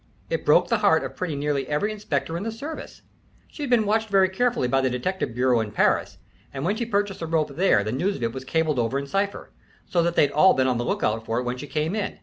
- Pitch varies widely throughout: Yes, wide, 7.5 semitones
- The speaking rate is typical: No, fast, 260 wpm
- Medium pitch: Yes, medium, 160 Hz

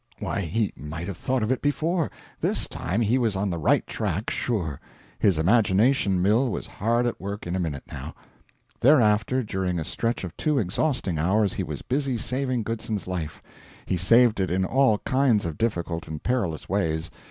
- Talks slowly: No, average, 185 wpm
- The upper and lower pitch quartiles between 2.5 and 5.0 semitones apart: No, wide, 5.5 semitones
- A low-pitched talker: Yes, low, 105 Hz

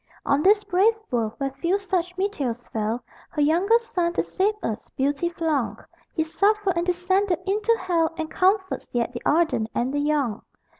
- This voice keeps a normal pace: Yes, average, 170 wpm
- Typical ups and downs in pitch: No, wide, 5.8 semitones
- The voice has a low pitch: No, very high, 340 Hz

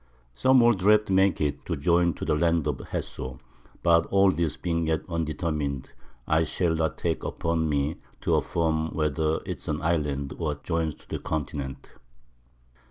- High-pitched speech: No, very low, 80 Hz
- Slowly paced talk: No, average, 165 wpm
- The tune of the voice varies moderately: No, narrow, 2.3 semitones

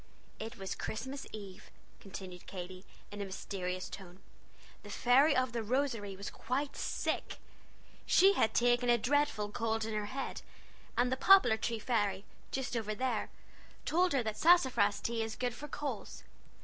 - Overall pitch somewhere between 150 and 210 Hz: No, high, 225 Hz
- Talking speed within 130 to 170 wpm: Yes, average, 160 wpm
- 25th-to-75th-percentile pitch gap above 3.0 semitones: Yes, average, 4.2 semitones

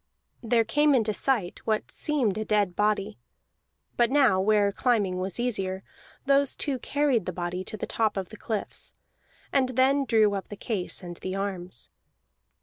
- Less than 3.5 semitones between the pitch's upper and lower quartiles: No, average, 4.6 semitones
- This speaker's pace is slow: No, average, 165 wpm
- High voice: Yes, high, 215 Hz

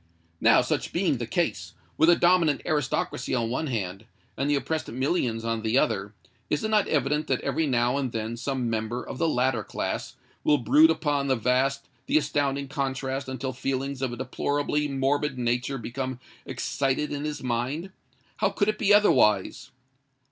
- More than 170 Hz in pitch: No, low, 135 Hz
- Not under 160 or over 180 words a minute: Yes, average, 170 wpm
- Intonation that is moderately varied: Yes, average, 3.4 semitones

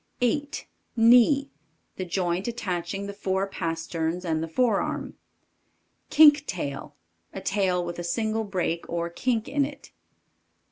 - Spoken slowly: Yes, slow, 130 wpm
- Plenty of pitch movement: Yes, wide, 5.7 semitones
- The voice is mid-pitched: No, high, 195 Hz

